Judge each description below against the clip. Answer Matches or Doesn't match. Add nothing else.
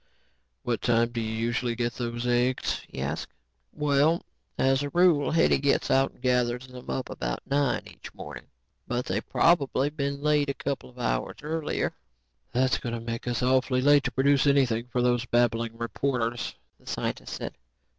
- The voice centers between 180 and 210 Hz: Doesn't match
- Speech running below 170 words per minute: Doesn't match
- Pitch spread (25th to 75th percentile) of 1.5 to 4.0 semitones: Matches